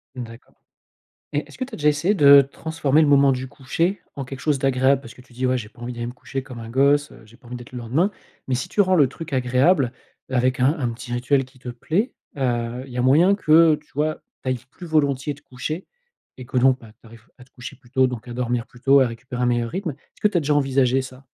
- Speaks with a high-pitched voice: No, low, 130 Hz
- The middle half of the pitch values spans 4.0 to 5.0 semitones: No, average, 2.9 semitones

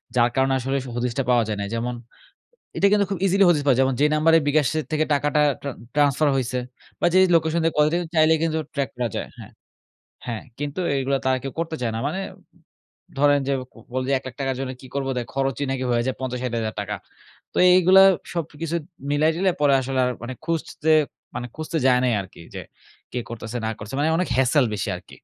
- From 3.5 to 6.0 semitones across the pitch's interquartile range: Yes, average, 4.0 semitones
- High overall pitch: No, low, 135 Hz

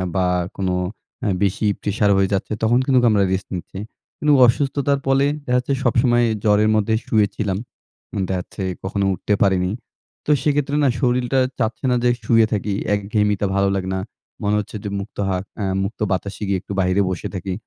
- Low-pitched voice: Yes, low, 105 Hz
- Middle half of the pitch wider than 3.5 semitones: Yes, average, 4.0 semitones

